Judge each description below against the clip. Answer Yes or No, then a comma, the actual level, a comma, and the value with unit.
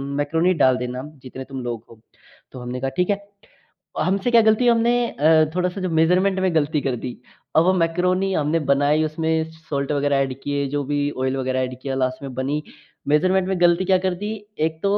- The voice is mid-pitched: Yes, medium, 155 Hz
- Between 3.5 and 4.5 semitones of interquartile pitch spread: No, average, 5.3 semitones